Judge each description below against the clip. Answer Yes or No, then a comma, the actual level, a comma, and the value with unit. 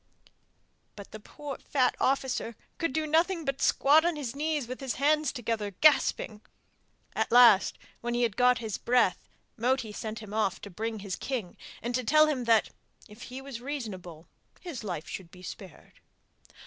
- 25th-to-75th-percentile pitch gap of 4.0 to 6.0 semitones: Yes, average, 4.6 semitones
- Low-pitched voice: No, high, 245 Hz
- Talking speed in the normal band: Yes, average, 170 wpm